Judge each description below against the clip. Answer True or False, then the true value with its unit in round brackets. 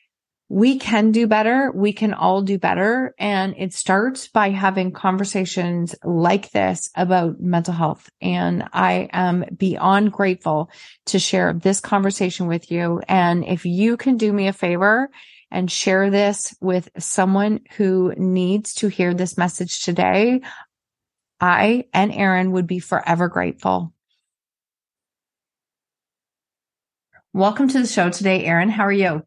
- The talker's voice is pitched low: False (190 Hz)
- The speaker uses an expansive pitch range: False (2.5 semitones)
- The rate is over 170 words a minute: False (135 wpm)